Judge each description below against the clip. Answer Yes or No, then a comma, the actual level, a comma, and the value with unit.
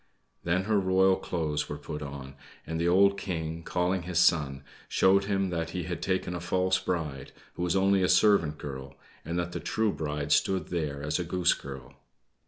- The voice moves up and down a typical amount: Yes, average, 3.8 semitones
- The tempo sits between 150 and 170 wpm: No, average, 190 wpm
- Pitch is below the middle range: Yes, very low, 85 Hz